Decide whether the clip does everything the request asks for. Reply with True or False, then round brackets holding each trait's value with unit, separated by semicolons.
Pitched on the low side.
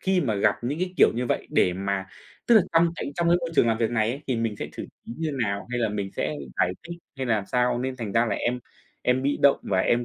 True (120 Hz)